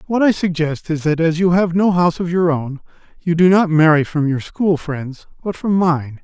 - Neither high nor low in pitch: Yes, medium, 165 Hz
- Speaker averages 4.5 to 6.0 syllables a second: Yes, 4.9 syllables/s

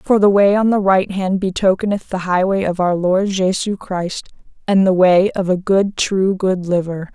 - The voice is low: No, high, 190 Hz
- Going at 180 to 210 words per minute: Yes, average, 200 wpm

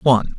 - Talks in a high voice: No, low, 125 Hz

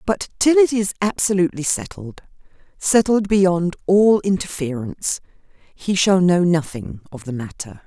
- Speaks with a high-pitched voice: No, medium, 175 Hz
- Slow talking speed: Yes, slow, 120 wpm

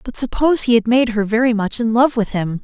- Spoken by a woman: Yes, female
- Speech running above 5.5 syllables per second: Yes, 5.9 syllables/s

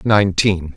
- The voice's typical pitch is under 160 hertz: Yes, very low, 95 Hz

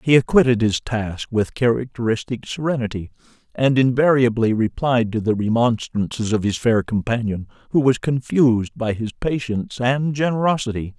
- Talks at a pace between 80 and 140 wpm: Yes, slow, 135 wpm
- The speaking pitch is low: Yes, low, 120 Hz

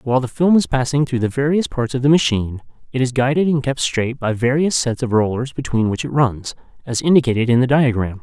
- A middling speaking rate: No, fast, 235 wpm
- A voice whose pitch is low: Yes, low, 130 Hz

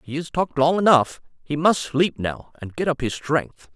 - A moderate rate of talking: No, fast, 225 wpm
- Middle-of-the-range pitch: Yes, medium, 150 Hz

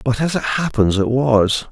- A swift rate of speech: Yes, fast, 210 wpm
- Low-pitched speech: Yes, low, 125 Hz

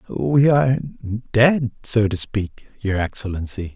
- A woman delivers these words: No, male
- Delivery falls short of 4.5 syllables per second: Yes, 4.0 syllables/s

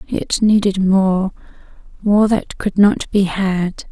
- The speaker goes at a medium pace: No, slow, 125 wpm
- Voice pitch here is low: No, high, 195 Hz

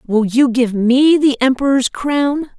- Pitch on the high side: Yes, very high, 260 Hz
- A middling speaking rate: Yes, average, 160 wpm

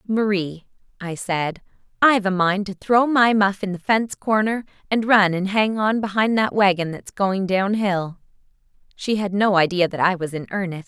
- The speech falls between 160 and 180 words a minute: No, average, 195 wpm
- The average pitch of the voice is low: No, high, 195 Hz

